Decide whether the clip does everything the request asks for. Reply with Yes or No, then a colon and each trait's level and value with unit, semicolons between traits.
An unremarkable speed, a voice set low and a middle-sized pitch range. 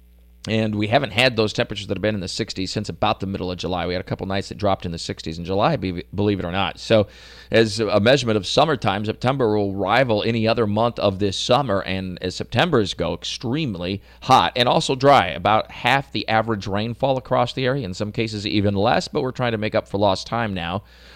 No: fast, 230 wpm; low, 105 Hz; average, 3.3 semitones